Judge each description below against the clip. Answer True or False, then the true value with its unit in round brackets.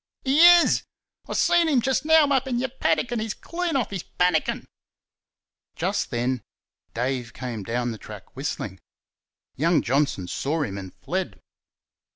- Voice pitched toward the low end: False (160 Hz)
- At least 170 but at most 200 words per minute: False (155 wpm)